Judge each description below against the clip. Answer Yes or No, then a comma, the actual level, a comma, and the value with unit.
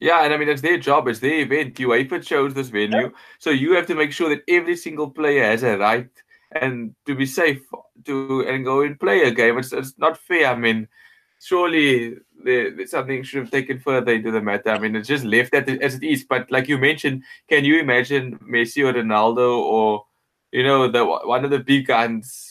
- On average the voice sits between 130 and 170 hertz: Yes, low, 135 Hz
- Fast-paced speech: Yes, fast, 225 wpm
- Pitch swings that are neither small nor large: Yes, average, 3.5 semitones